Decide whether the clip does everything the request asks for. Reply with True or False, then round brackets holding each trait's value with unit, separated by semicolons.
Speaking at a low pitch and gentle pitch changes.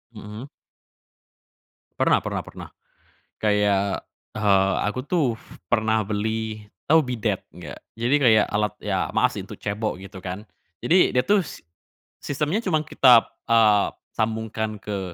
False (110 Hz; 3.5 semitones)